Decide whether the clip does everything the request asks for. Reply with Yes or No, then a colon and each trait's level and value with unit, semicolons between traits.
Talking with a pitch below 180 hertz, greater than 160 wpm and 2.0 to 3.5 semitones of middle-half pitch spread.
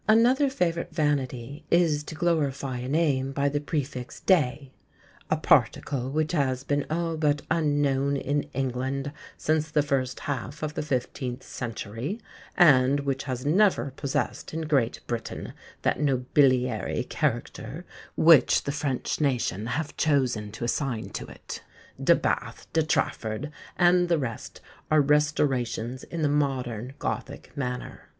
No: medium, 140 Hz; average, 140 wpm; average, 3.2 semitones